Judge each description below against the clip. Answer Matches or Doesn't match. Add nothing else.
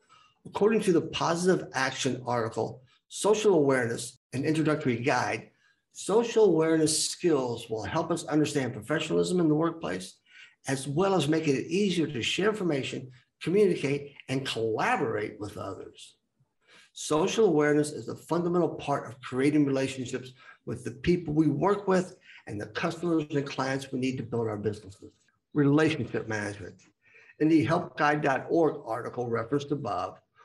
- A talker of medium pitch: Matches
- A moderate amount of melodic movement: Matches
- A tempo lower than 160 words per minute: Matches